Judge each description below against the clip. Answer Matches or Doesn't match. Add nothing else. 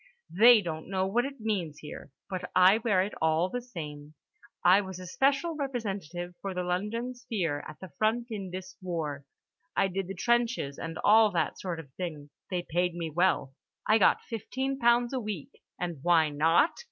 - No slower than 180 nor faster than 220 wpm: Matches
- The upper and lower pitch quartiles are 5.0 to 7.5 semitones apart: Matches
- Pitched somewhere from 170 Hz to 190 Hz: Matches